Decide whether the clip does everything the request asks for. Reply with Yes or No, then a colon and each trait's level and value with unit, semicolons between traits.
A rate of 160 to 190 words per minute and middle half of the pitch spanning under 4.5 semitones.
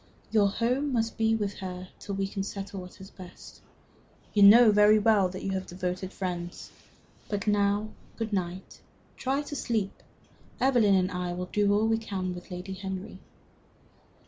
Yes: average, 170 wpm; average, 2.7 semitones